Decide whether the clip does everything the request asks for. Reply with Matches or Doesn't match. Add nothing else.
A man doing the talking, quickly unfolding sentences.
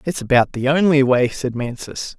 Doesn't match